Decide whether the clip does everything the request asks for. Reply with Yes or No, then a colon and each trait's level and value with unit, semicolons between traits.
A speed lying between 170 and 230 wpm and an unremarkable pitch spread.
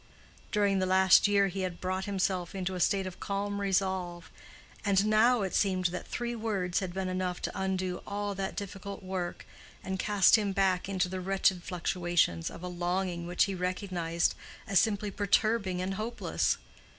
No: average, 175 wpm; narrow, 1.8 semitones